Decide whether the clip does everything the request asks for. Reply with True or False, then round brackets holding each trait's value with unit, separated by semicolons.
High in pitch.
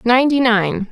True (235 Hz)